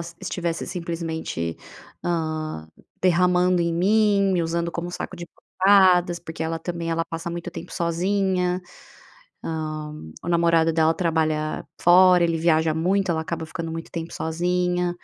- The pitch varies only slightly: Yes, narrow, 1.7 semitones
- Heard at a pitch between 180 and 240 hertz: No, medium, 170 Hz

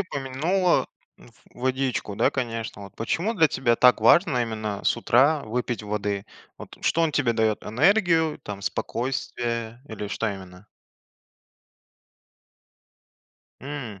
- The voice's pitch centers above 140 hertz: No, low, 120 Hz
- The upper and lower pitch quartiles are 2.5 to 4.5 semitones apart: No, average, 5.0 semitones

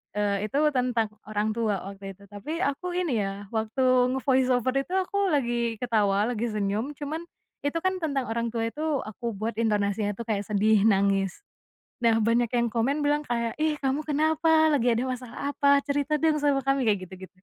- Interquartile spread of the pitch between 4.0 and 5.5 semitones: Yes, average, 5.1 semitones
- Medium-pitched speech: No, high, 235 Hz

